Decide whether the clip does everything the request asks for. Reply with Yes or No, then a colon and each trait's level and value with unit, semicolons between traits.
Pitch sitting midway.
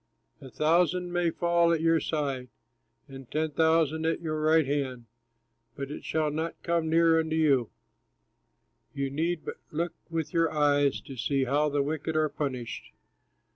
Yes: medium, 155 Hz